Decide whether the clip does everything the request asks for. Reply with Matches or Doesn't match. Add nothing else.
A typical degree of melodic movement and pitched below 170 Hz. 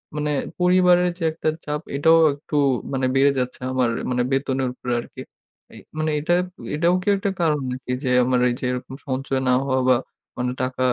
Matches